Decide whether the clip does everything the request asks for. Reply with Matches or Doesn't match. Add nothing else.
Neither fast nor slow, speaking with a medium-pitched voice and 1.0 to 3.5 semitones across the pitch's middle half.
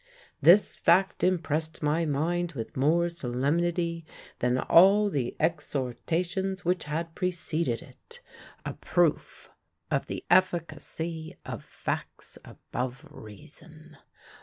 Doesn't match